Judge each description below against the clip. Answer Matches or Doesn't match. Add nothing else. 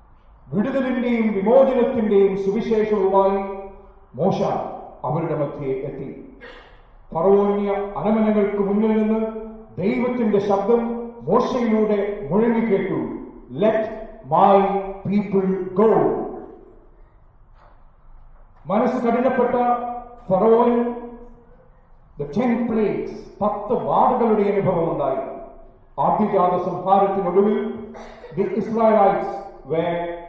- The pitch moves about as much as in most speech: Matches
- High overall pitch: Matches